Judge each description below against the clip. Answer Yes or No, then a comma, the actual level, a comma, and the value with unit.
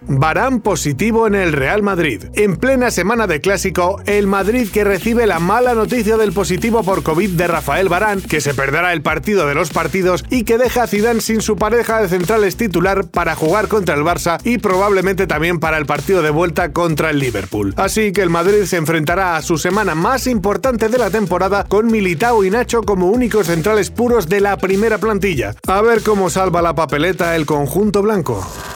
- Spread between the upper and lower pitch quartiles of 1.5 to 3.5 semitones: No, average, 4.1 semitones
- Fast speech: Yes, fast, 200 wpm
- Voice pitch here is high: Yes, high, 195 Hz